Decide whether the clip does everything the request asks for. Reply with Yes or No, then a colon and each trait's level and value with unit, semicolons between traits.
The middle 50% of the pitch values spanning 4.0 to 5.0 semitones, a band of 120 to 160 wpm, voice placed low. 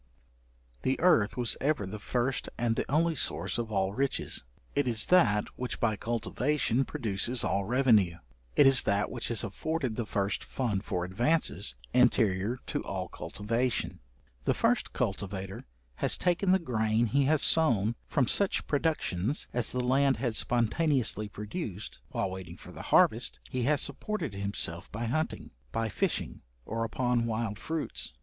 Yes: average, 4.6 semitones; average, 155 wpm; low, 115 Hz